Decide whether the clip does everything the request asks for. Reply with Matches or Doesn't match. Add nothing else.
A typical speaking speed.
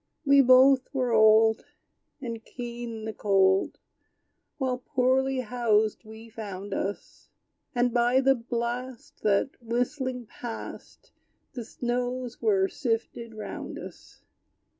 Doesn't match